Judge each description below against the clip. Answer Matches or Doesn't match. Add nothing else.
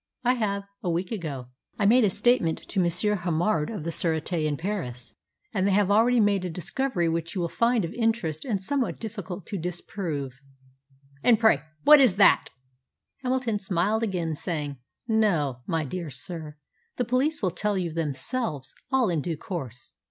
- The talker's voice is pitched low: Doesn't match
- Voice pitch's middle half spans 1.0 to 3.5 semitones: Doesn't match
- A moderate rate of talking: Matches